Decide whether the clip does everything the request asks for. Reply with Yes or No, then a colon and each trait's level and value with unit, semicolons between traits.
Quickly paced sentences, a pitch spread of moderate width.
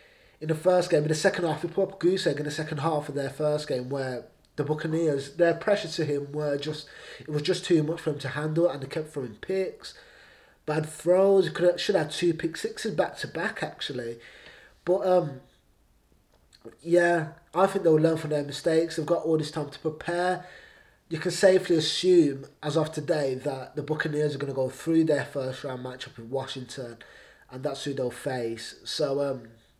Yes: fast, 210 wpm; average, 3.4 semitones